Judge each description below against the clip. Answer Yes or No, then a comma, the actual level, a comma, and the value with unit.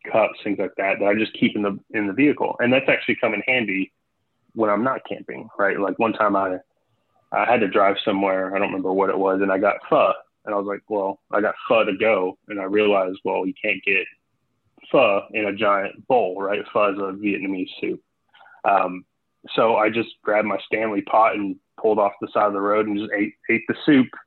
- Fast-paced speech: Yes, fast, 230 wpm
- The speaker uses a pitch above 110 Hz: No, low, 100 Hz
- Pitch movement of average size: No, narrow, 1.7 semitones